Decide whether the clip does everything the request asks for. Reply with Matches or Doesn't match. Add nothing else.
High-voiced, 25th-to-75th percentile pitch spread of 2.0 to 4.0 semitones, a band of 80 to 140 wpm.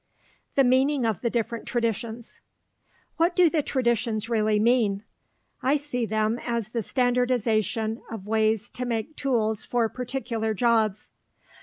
Matches